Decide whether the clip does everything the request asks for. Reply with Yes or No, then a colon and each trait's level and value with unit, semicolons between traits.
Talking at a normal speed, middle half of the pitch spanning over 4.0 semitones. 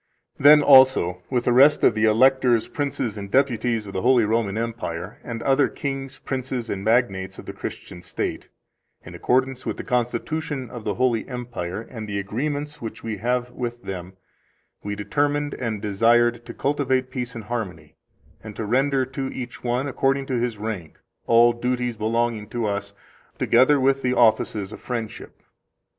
No: average, 170 wpm; average, 3.4 semitones